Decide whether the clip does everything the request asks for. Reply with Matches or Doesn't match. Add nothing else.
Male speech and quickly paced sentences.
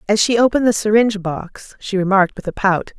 Doesn't match